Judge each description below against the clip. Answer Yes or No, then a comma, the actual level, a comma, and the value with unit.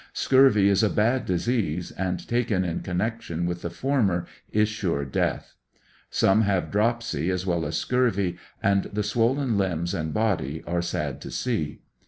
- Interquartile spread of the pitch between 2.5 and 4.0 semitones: No, average, 4.6 semitones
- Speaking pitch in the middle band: No, low, 100 Hz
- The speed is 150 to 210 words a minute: Yes, average, 165 wpm